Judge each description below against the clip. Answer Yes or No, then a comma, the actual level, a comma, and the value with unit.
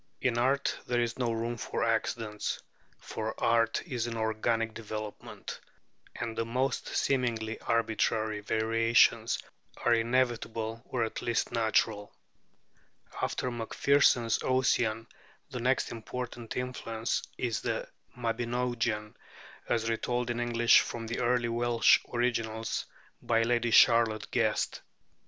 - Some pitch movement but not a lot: No, narrow, 1.4 semitones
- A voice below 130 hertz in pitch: Yes, low, 115 Hz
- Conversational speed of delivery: No, slow, 115 wpm